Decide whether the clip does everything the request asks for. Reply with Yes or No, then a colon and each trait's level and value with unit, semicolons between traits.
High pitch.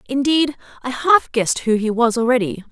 Yes: high, 245 Hz